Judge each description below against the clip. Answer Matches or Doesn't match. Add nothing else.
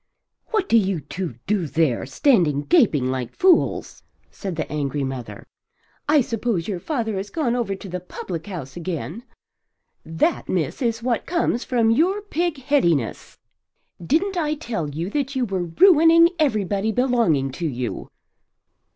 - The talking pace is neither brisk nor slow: Matches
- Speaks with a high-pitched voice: Matches